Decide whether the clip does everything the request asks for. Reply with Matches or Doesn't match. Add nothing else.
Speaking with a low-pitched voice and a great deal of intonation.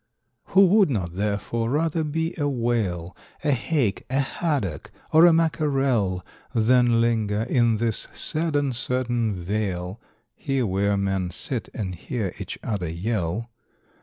Matches